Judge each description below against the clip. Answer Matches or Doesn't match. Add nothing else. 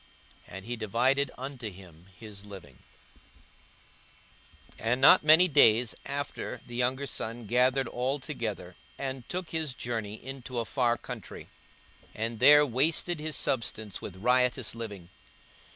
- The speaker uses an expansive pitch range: Doesn't match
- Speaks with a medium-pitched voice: Doesn't match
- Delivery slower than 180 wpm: Matches